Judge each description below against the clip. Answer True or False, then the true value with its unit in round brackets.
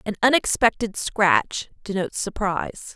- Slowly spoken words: True (100 wpm)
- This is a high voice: True (205 Hz)